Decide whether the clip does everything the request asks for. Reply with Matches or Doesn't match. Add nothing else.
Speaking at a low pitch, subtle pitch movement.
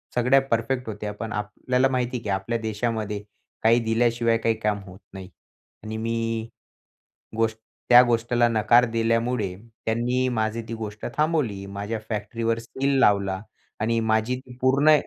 Matches